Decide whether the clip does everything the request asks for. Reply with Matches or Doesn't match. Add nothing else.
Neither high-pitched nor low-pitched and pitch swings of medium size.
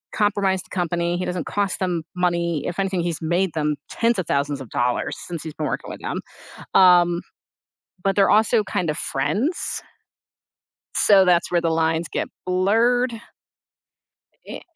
Matches